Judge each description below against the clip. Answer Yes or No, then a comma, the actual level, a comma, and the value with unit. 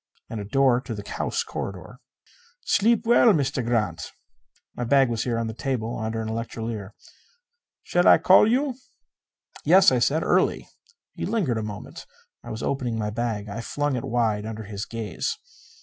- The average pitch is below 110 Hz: No, low, 115 Hz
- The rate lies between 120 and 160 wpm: No, average, 170 wpm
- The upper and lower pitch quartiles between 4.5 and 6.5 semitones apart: No, average, 3.7 semitones